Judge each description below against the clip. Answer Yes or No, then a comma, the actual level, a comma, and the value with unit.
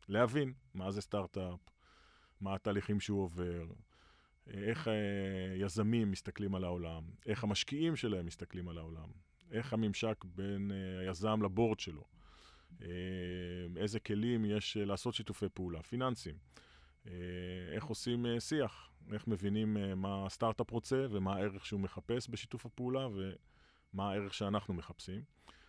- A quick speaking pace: No, average, 115 wpm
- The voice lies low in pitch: Yes, low, 100 Hz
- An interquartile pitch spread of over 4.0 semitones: No, average, 3.6 semitones